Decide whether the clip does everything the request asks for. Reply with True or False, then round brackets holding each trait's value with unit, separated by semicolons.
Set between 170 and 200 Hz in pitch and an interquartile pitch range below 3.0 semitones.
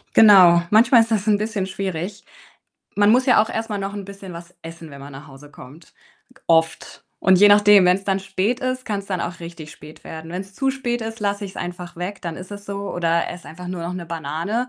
False (190 Hz; 3.6 semitones)